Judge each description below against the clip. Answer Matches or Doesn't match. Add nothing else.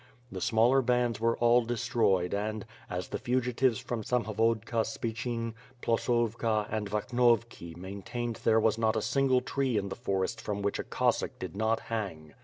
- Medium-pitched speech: Doesn't match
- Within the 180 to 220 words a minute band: Doesn't match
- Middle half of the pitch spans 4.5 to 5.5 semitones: Doesn't match